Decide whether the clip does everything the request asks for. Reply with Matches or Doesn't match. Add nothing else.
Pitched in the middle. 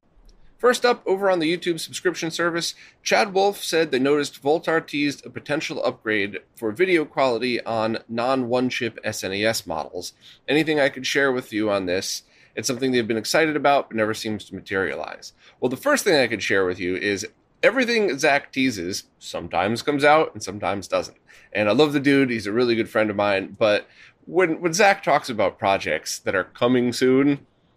Doesn't match